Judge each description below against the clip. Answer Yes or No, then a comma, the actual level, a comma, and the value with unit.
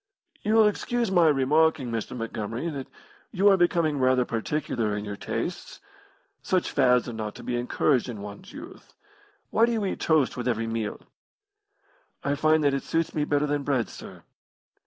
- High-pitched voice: No, medium, 140 Hz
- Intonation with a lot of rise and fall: Yes, wide, 5.9 semitones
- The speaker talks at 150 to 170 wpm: No, average, 180 wpm